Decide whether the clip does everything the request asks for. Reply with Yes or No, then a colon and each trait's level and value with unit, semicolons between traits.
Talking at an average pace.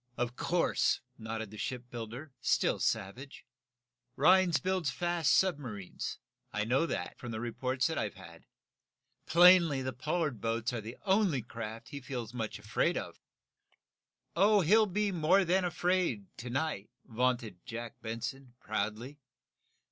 No: slow, 130 wpm